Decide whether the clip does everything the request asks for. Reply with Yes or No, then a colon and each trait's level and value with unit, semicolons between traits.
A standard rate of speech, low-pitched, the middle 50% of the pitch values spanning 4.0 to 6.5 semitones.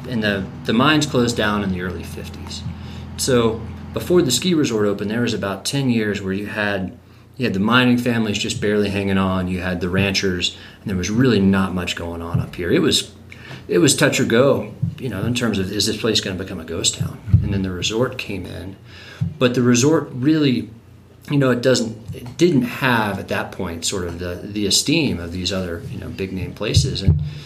No: fast, 220 wpm; low, 105 Hz; average, 4.4 semitones